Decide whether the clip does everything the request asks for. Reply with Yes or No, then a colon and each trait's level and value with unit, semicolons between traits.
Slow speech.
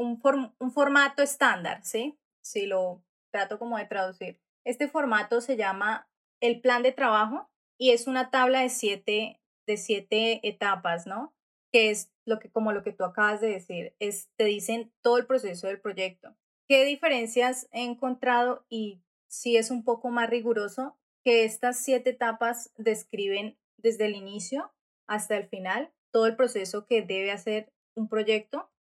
No: average, 170 wpm